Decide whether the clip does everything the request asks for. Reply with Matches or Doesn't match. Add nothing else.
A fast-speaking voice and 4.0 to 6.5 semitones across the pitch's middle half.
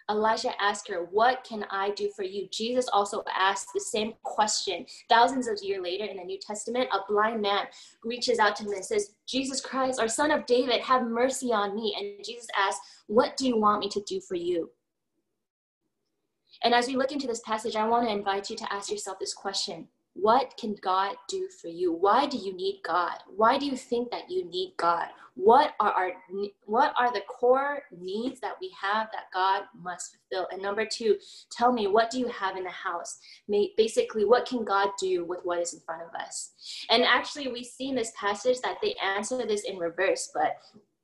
Matches